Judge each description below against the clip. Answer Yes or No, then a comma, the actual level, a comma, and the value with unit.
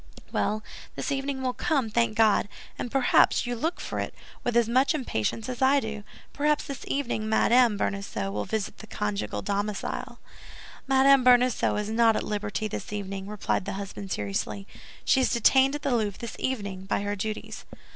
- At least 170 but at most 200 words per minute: Yes, average, 175 wpm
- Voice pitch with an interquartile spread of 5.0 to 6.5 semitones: No, average, 4.3 semitones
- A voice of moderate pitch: No, high, 220 Hz